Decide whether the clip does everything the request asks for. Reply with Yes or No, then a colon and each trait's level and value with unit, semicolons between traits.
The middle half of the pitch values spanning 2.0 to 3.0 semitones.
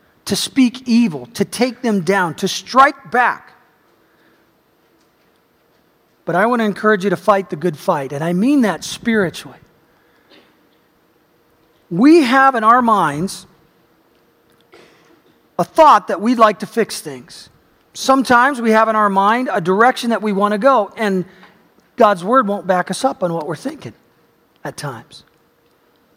No: average, 4.4 semitones